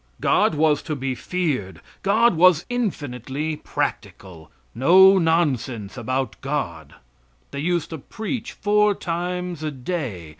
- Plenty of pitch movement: Yes, wide, 5.8 semitones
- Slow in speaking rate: Yes, slow, 120 wpm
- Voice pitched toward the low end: No, medium, 155 Hz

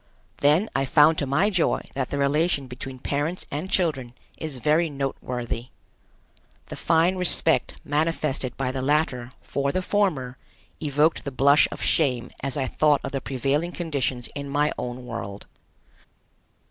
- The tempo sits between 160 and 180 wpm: No, average, 150 wpm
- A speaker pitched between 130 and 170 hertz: Yes, medium, 140 Hz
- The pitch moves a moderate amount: Yes, average, 3.4 semitones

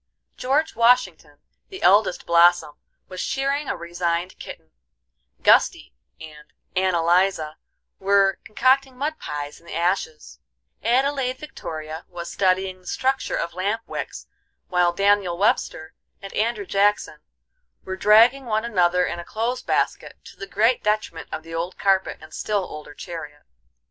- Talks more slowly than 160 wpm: Yes, average, 140 wpm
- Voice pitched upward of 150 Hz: Yes, high, 190 Hz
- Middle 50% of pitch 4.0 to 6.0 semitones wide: Yes, average, 4.8 semitones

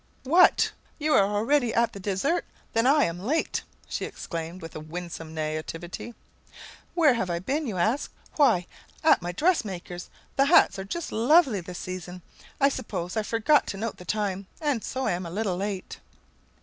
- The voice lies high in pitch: Yes, high, 205 Hz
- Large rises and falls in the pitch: Yes, wide, 7.2 semitones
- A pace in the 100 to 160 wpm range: No, average, 175 wpm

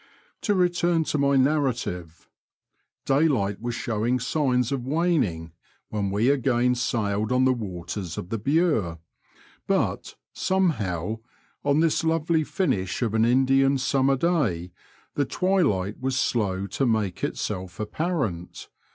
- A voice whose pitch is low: Yes, low, 125 Hz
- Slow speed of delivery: Yes, slow, 125 wpm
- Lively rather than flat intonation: Yes, wide, 6.3 semitones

